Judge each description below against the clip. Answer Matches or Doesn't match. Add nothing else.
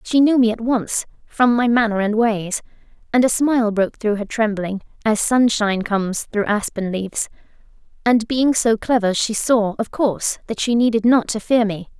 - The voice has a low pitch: Doesn't match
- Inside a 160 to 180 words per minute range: Doesn't match